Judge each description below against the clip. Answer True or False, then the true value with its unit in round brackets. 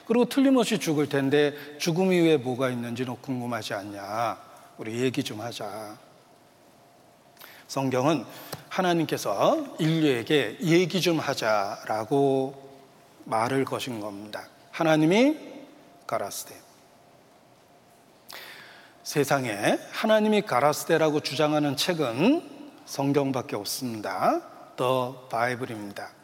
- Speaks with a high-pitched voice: False (145 Hz)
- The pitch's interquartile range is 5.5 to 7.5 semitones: True (6.2 semitones)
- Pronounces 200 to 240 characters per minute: True (235 characters per minute)